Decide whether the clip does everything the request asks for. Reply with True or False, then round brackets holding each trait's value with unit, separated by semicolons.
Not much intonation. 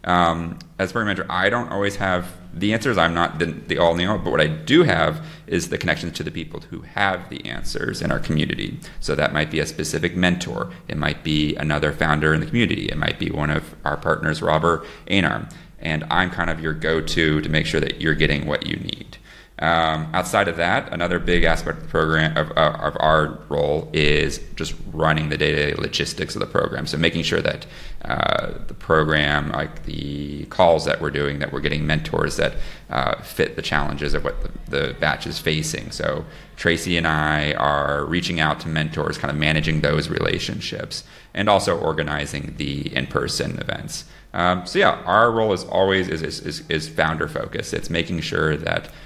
True (2.3 semitones)